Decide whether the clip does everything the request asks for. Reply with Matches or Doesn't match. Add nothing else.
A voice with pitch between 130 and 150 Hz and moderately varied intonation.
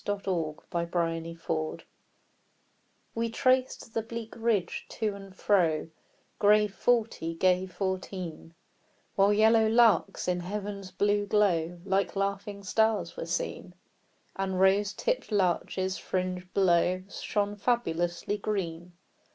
Doesn't match